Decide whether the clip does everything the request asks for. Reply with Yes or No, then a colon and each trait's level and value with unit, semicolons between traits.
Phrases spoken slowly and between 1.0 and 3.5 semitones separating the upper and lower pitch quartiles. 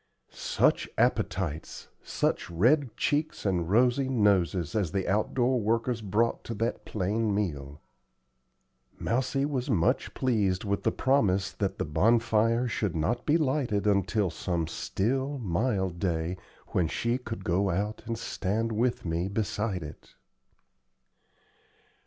No: slow, 130 wpm; average, 4.5 semitones